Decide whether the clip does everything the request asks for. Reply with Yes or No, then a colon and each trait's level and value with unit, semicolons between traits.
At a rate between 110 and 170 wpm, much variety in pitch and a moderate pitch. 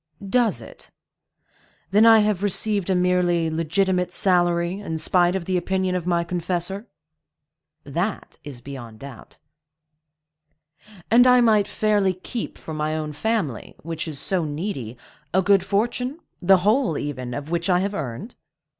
No: average, 145 wpm; average, 4.2 semitones; medium, 180 Hz